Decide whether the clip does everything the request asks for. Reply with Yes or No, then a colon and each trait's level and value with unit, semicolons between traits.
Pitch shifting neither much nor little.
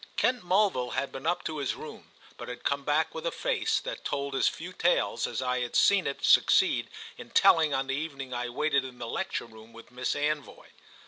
Yes: average, 3.9 semitones